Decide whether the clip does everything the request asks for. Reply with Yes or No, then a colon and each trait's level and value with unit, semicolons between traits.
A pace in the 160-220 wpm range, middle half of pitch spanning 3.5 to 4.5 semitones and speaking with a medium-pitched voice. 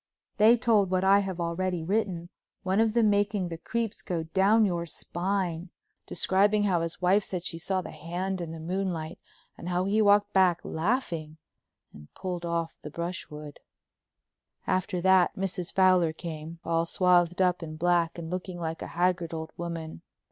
No: average, 170 wpm; narrow, 2.5 semitones; medium, 180 Hz